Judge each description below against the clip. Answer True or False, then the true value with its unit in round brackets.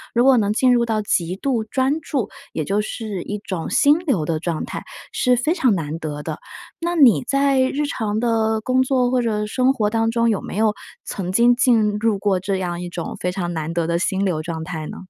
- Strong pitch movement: True (5.9 semitones)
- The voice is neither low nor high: False (215 Hz)